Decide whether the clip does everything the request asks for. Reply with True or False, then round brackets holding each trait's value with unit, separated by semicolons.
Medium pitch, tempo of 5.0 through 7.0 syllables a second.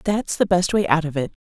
True (170 Hz; 5.7 syllables/s)